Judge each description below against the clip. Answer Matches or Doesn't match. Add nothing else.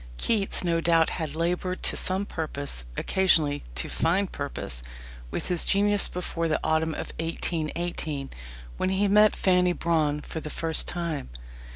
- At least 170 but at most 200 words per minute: Doesn't match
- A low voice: Doesn't match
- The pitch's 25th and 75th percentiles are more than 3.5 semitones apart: Doesn't match